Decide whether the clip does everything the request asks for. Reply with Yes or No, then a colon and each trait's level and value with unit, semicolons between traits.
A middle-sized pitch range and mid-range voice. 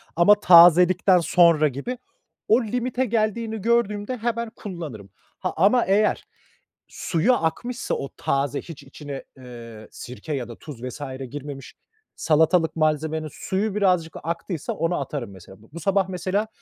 No: wide, 6.1 semitones; medium, 170 Hz